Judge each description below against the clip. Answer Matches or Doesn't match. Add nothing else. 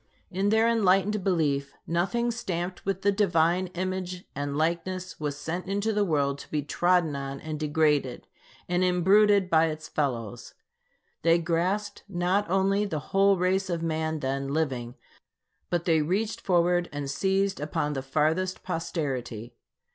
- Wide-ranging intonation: Doesn't match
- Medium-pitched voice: Matches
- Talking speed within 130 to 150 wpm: Matches